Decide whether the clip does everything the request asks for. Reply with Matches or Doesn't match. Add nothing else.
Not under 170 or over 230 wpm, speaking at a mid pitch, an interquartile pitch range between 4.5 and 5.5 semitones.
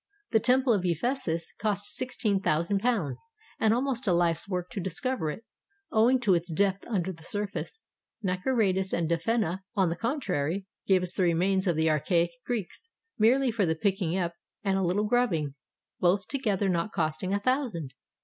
Doesn't match